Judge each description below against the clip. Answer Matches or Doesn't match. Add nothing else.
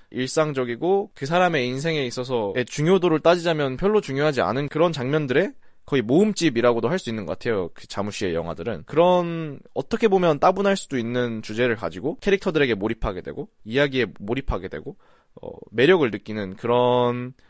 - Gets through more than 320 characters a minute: Matches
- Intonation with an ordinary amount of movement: Doesn't match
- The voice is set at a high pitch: Doesn't match